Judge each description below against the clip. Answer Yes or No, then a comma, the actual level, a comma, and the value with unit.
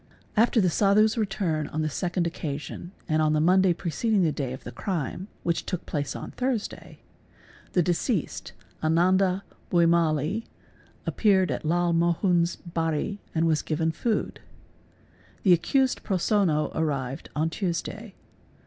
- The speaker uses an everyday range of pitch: Yes, average, 3.7 semitones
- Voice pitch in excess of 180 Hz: No, medium, 170 Hz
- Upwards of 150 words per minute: No, average, 140 wpm